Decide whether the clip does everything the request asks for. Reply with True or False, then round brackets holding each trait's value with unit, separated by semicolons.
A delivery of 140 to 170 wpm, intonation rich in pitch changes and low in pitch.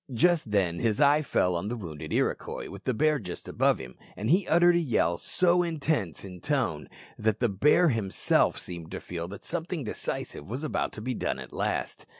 False (195 wpm; 8.9 semitones; 115 Hz)